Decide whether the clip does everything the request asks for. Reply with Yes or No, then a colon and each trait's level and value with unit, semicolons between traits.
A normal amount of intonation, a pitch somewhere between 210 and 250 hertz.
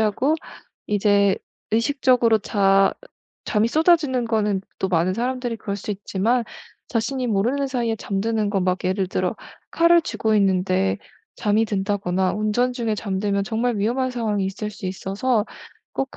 Yes: average, 3.8 semitones; high, 215 Hz